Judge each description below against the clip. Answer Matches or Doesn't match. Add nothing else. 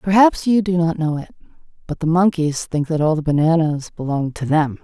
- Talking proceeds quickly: Matches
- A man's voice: Doesn't match